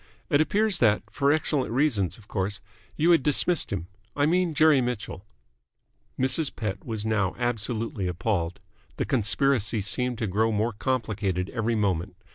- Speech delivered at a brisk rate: No, average, 150 wpm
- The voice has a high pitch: No, low, 115 Hz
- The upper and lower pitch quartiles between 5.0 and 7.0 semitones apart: Yes, wide, 5.5 semitones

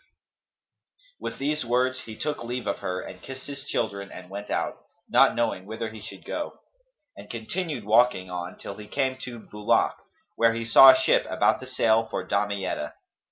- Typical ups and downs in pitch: Yes, average, 4.1 semitones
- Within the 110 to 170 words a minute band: No, average, 190 wpm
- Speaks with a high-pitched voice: No, low, 115 Hz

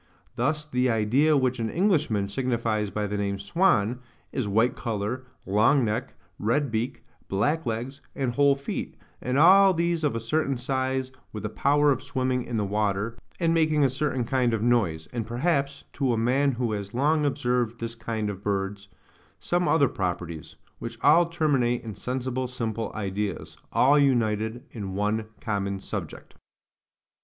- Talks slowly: No, average, 165 wpm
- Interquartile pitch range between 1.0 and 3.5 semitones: No, average, 4.6 semitones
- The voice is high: No, low, 120 Hz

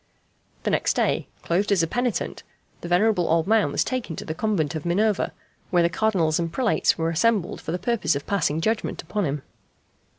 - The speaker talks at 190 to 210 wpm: Yes, average, 195 wpm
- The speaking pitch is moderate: Yes, medium, 175 Hz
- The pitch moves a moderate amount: Yes, average, 4.9 semitones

